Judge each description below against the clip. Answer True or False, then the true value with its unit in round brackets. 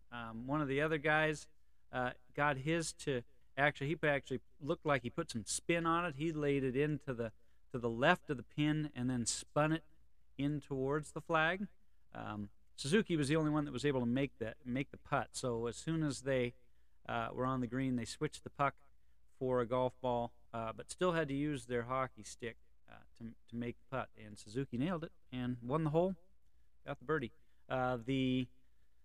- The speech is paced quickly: True (210 wpm)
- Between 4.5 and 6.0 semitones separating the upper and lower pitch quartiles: False (4.1 semitones)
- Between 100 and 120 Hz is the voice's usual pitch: False (130 Hz)